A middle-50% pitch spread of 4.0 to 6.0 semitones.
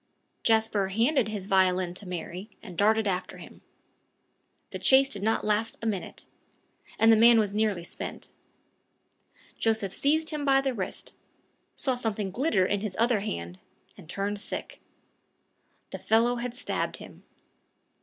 No: average, 3.5 semitones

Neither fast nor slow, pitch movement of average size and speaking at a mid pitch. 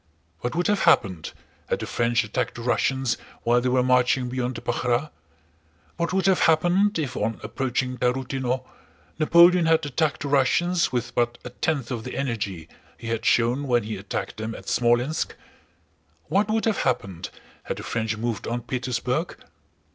No: average, 170 wpm; average, 4.3 semitones; low, 125 Hz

